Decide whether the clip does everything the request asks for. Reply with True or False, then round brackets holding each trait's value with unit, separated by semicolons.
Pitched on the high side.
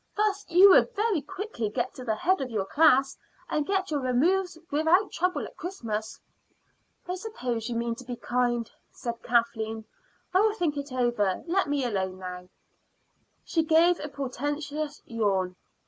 True (280 Hz)